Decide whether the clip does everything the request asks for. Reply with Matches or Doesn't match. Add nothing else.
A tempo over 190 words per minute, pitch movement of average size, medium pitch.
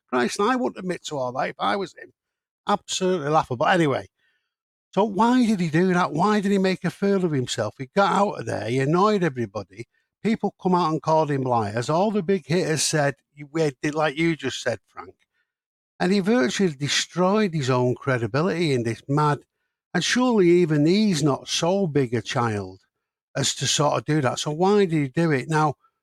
Doesn't match